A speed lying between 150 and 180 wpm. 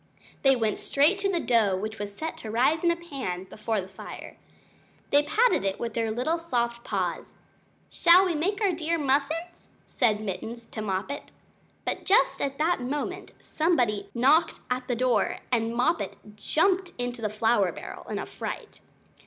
Yes: average, 175 wpm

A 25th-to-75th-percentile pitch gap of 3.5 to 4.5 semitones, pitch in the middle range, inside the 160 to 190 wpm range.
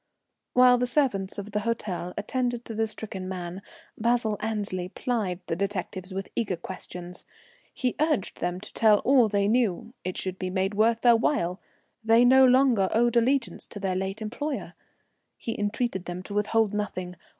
No: average, 4.1 semitones; high, 210 Hz; average, 170 wpm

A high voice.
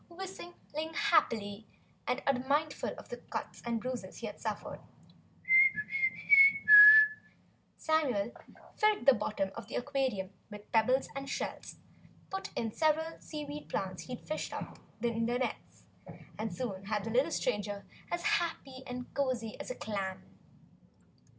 Yes: very high, 250 Hz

